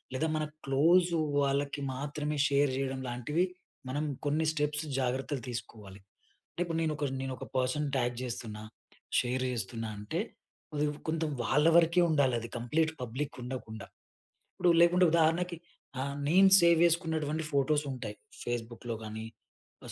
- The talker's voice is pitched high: No, medium, 140 Hz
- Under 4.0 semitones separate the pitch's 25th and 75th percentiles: No, average, 4.5 semitones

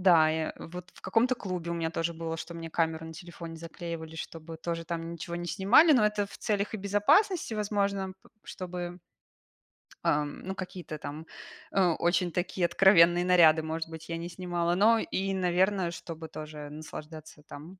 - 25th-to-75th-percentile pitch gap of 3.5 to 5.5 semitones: No, average, 2.8 semitones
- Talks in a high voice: No, medium, 170 Hz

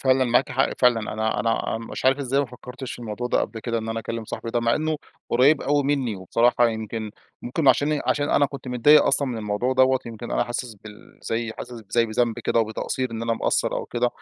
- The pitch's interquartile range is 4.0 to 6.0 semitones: No, narrow, 2.6 semitones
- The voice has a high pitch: No, low, 120 Hz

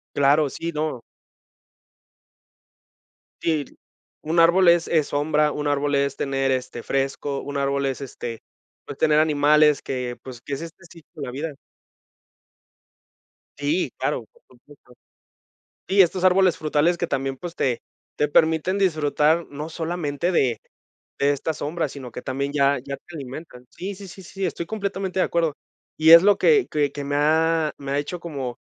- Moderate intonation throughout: Yes, average, 3.4 semitones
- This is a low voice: No, medium, 150 Hz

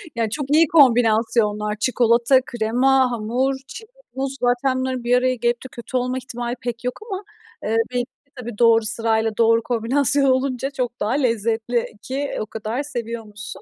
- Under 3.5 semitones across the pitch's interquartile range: Yes, narrow, 2.4 semitones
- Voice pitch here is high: Yes, high, 240 Hz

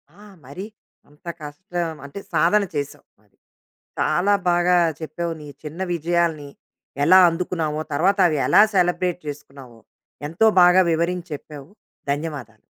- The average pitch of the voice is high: No, medium, 165 Hz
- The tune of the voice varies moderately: Yes, average, 3.2 semitones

